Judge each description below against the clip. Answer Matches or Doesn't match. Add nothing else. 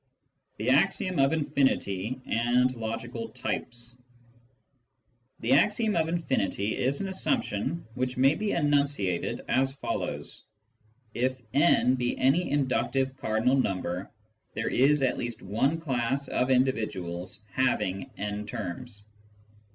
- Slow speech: Matches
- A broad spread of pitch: Doesn't match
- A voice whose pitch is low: Matches